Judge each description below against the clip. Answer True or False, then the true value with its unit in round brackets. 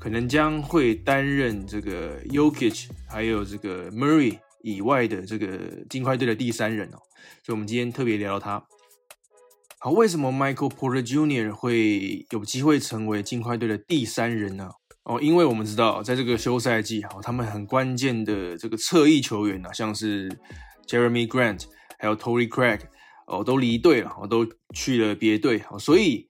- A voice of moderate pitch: False (115 Hz)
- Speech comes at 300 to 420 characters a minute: True (330 characters per minute)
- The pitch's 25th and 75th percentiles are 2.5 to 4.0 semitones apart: True (3.5 semitones)